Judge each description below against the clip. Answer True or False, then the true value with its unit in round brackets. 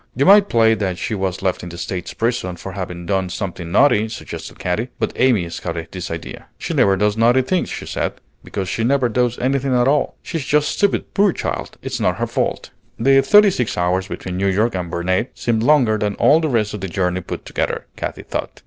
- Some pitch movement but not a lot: False (5.9 semitones)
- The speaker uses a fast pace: True (220 wpm)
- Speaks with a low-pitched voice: True (110 Hz)